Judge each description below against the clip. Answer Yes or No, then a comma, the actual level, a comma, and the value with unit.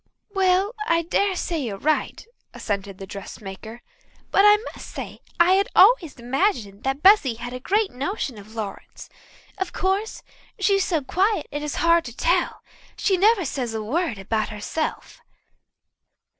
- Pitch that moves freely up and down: Yes, wide, 9.0 semitones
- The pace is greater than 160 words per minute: No, average, 155 wpm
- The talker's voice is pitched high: Yes, very high, 310 Hz